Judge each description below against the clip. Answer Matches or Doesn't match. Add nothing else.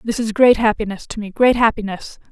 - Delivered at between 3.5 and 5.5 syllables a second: Doesn't match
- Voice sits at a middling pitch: Doesn't match